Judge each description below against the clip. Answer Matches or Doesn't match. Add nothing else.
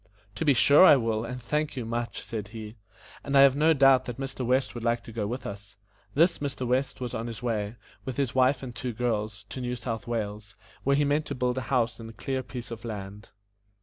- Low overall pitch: Matches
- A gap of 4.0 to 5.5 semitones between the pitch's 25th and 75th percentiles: Doesn't match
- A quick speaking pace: Matches